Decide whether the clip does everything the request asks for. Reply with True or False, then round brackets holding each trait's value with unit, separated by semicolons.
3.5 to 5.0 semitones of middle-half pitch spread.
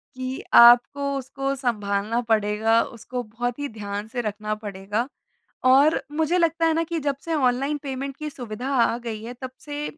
True (4.3 semitones)